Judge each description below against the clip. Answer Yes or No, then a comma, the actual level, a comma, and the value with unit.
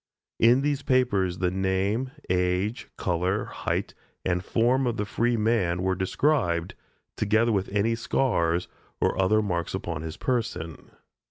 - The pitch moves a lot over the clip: No, average, 4.5 semitones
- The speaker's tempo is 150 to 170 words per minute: No, average, 140 wpm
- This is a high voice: No, low, 100 Hz